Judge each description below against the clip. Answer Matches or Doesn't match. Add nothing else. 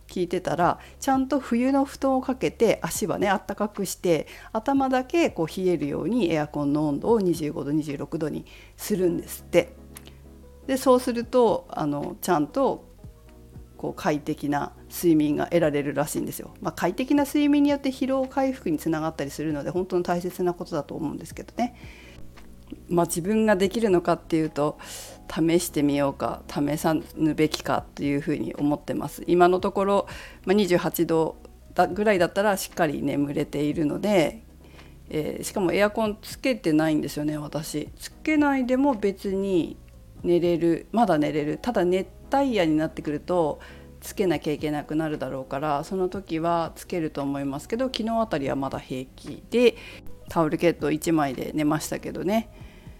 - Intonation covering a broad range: Matches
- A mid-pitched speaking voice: Matches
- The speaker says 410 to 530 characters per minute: Doesn't match